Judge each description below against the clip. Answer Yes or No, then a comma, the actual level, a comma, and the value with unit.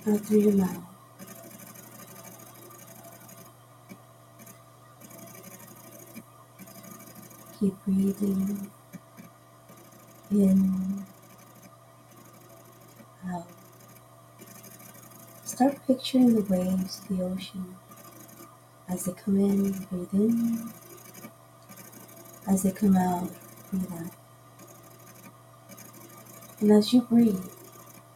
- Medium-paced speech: No, slow, 65 wpm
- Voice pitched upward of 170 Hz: Yes, high, 190 Hz